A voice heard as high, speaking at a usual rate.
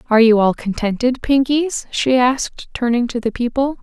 Yes: high, 245 Hz; average, 170 wpm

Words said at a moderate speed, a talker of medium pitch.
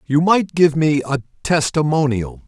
Yes: average, 145 wpm; medium, 150 Hz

